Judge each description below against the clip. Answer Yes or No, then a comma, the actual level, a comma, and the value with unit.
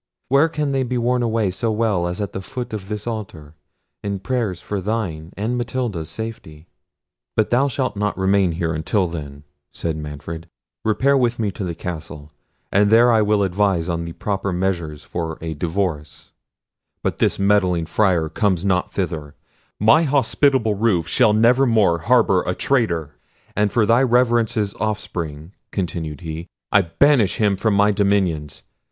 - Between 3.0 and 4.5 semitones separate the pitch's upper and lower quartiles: No, average, 5.2 semitones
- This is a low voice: Yes, low, 100 Hz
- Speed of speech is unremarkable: Yes, average, 160 wpm